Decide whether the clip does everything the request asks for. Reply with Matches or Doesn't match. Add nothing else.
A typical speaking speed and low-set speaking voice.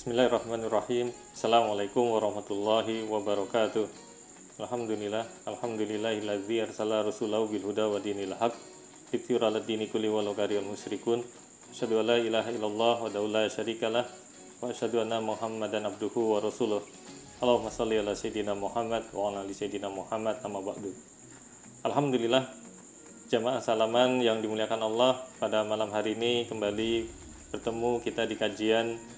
Matches